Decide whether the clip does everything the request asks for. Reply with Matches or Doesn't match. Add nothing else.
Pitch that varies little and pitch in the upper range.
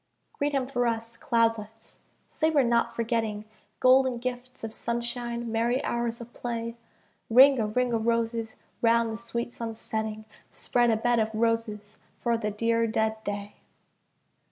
Matches